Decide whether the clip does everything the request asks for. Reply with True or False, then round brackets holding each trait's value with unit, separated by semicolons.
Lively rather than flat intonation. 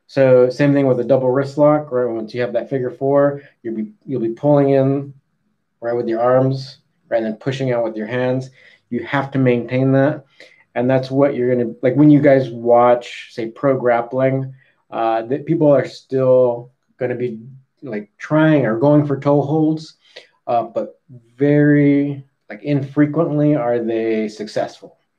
False (2.8 semitones)